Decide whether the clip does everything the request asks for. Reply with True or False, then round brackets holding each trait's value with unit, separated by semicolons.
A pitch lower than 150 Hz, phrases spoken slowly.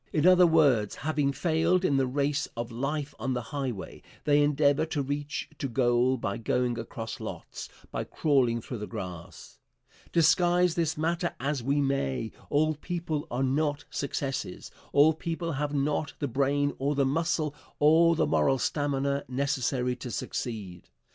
False (140 Hz; 155 wpm)